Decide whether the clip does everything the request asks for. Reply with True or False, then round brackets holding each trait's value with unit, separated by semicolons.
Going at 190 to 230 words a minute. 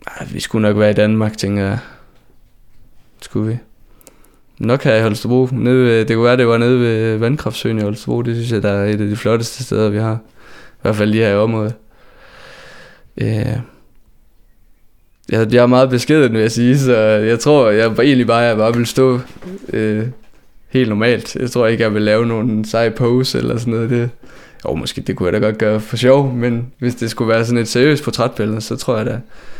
True (200 wpm)